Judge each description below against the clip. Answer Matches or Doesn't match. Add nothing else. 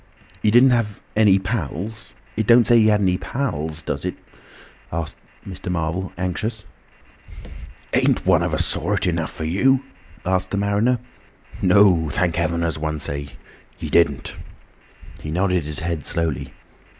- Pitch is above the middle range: Doesn't match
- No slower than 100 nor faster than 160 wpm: Matches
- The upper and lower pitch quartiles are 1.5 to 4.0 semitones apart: Doesn't match